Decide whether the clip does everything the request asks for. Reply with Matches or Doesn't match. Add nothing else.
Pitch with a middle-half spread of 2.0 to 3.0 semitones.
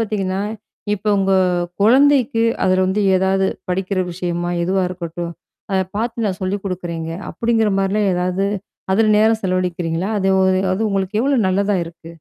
Matches